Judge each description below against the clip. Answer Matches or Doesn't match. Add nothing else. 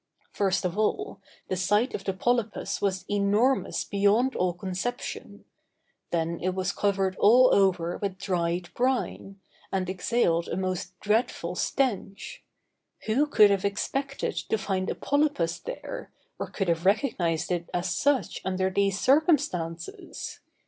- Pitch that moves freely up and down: Doesn't match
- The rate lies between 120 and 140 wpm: Matches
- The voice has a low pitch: Doesn't match